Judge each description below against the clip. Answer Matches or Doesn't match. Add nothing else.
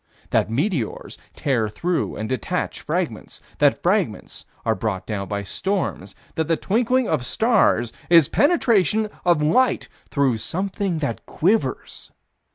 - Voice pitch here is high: Doesn't match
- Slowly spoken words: Matches